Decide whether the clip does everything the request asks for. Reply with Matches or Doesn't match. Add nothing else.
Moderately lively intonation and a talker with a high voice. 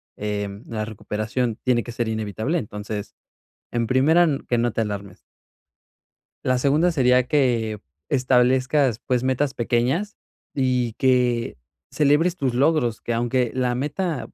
Doesn't match